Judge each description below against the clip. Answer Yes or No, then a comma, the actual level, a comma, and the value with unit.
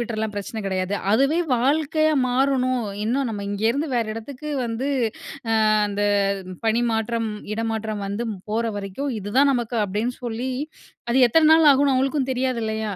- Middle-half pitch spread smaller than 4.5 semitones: Yes, average, 3.6 semitones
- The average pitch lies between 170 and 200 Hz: No, high, 235 Hz